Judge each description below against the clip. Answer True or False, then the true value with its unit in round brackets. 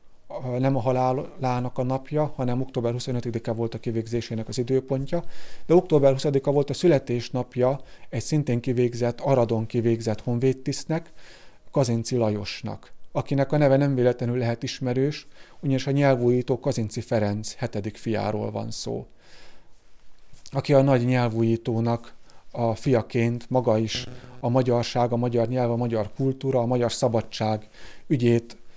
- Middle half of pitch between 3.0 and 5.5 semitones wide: False (2.5 semitones)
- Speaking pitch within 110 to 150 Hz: True (125 Hz)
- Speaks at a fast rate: False (130 wpm)